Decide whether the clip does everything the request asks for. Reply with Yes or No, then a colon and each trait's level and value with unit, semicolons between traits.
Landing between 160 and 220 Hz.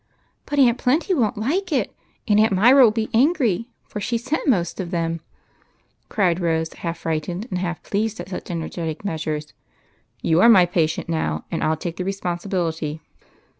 Yes: medium, 185 Hz